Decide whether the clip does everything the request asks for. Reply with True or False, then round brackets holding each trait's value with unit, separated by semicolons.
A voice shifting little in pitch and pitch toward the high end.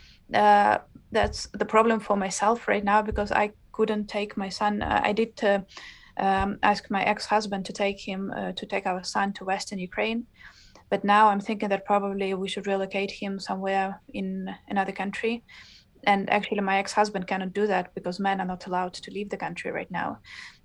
True (1.4 semitones; 200 Hz)